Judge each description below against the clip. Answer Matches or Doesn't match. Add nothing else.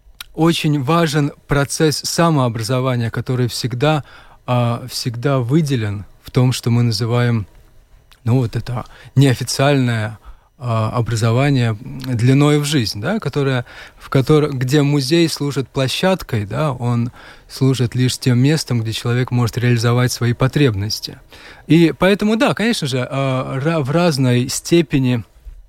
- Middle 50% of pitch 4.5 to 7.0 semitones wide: Doesn't match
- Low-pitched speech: Matches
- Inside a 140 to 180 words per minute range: Doesn't match